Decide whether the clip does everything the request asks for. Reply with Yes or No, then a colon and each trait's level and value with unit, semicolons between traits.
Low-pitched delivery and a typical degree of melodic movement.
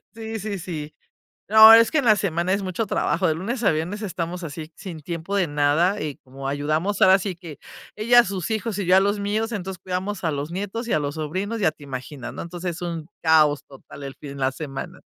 No: medium, 180 Hz; average, 4.8 semitones